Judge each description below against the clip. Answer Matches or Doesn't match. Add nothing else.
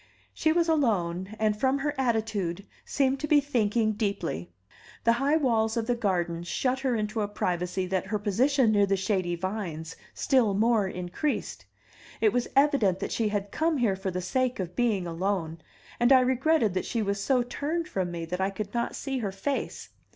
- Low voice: Doesn't match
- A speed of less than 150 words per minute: Doesn't match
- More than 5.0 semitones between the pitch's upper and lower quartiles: Matches